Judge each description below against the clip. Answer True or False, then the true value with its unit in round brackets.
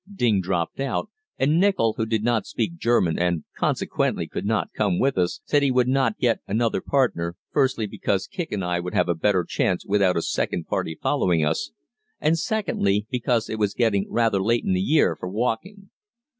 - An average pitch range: False (5.7 semitones)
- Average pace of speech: True (195 wpm)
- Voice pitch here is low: True (110 Hz)